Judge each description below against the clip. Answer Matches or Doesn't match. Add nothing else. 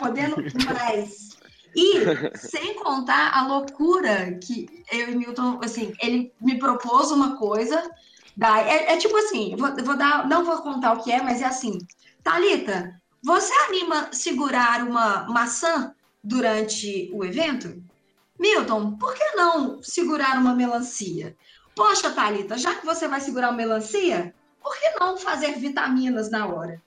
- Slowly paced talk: Doesn't match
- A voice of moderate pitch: Doesn't match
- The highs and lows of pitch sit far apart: Matches